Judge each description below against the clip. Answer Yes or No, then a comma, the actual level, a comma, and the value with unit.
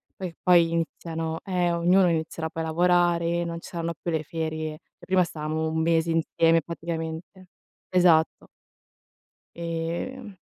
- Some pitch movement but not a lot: No, narrow, 1.4 semitones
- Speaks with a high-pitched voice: No, medium, 165 Hz